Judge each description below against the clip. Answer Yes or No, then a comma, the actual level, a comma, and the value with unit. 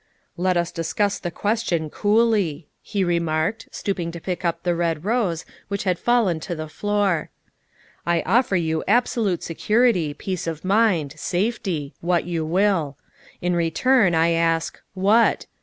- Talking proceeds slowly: No, average, 155 wpm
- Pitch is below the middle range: No, medium, 175 Hz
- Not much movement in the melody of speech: No, average, 3.8 semitones